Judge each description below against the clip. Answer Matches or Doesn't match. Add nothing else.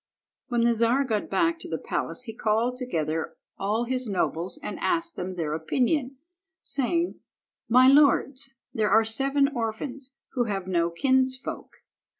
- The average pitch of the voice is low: Doesn't match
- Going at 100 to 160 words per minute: Matches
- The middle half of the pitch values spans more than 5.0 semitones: Doesn't match